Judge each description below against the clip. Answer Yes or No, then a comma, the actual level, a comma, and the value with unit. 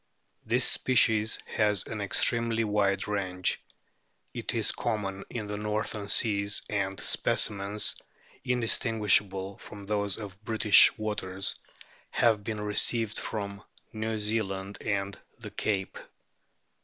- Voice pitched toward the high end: No, low, 105 Hz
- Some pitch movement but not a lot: No, narrow, 1.7 semitones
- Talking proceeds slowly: Yes, slow, 115 wpm